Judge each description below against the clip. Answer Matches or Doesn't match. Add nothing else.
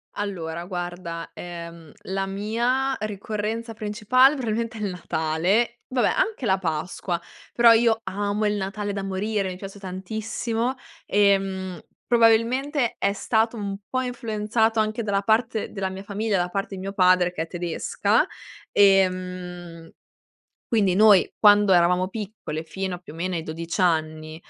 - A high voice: Matches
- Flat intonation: Doesn't match